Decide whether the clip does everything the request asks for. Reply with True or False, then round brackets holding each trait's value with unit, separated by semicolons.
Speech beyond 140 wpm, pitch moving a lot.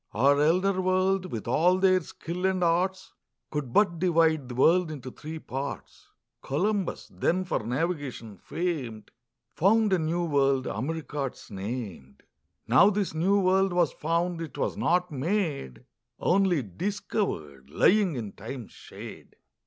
False (135 wpm; 6.0 semitones)